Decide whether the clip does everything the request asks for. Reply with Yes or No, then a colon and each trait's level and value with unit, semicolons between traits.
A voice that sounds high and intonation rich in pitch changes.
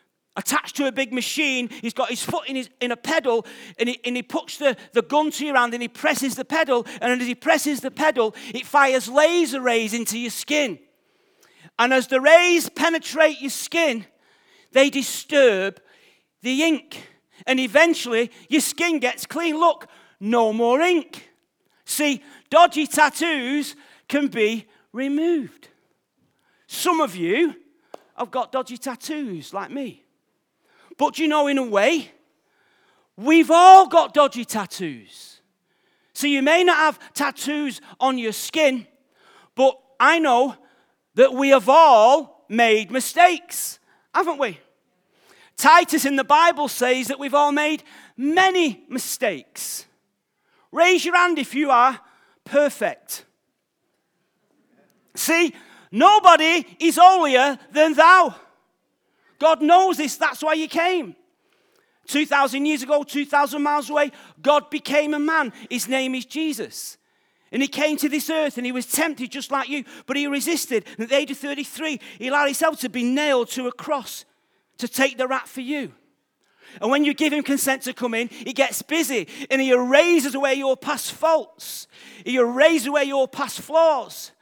No: very high, 285 Hz; average, 3.7 semitones